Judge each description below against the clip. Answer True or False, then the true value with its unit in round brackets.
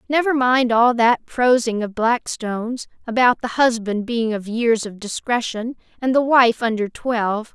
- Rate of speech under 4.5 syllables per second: True (4.3 syllables/s)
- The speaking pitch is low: False (235 Hz)